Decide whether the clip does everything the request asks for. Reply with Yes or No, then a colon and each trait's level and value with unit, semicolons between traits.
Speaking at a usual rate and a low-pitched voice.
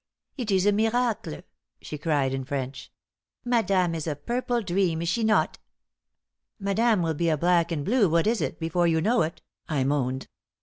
No: average, 180 wpm; medium, 175 Hz